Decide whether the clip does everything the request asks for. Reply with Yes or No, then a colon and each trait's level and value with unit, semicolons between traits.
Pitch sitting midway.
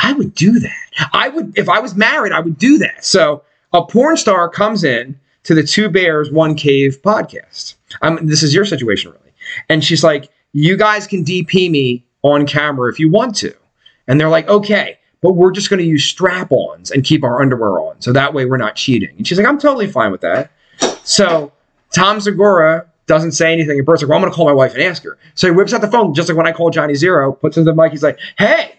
Yes: medium, 165 Hz